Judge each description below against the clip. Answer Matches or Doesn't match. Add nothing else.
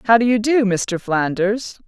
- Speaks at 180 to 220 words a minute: Doesn't match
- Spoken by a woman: Matches